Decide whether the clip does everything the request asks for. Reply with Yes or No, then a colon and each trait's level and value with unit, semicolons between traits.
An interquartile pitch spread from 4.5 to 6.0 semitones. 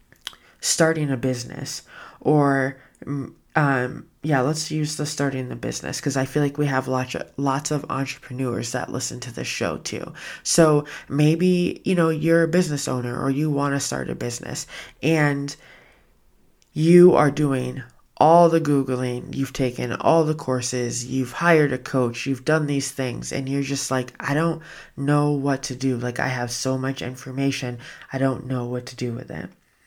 No: average, 2.7 semitones